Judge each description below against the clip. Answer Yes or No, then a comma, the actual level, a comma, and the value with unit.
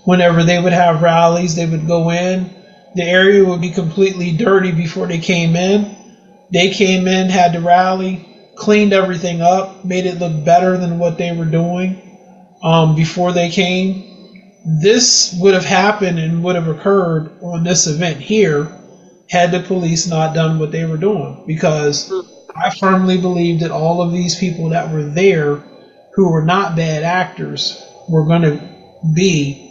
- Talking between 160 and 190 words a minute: Yes, average, 170 wpm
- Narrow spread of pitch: Yes, narrow, 2.1 semitones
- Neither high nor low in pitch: Yes, medium, 180 Hz